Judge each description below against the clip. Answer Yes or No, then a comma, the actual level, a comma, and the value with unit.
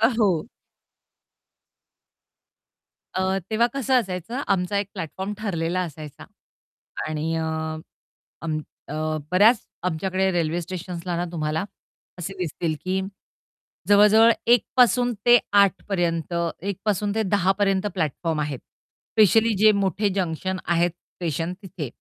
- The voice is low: No, medium, 185 Hz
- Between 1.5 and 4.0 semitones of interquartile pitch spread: Yes, average, 3.7 semitones